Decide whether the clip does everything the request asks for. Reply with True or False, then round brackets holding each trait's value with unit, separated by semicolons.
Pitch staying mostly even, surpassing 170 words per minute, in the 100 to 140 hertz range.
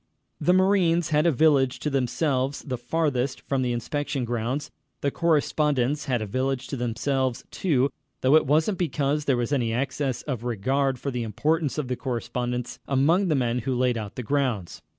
False (3.3 semitones; 180 wpm; 135 Hz)